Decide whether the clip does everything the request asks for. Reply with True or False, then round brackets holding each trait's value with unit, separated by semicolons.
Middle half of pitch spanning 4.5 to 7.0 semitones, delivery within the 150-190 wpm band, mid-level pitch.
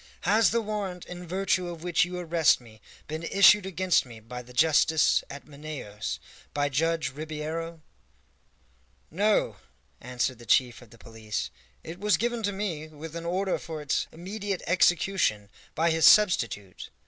True (5.1 semitones; 155 wpm; 165 Hz)